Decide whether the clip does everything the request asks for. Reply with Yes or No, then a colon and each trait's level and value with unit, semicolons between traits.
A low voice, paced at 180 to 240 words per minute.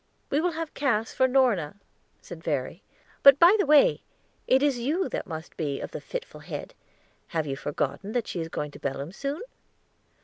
No: high, 225 Hz; average, 190 wpm